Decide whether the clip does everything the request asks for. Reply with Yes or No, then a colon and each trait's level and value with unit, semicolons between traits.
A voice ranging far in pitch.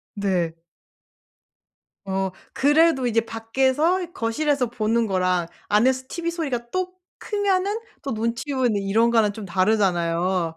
Yes: wide, 6.5 semitones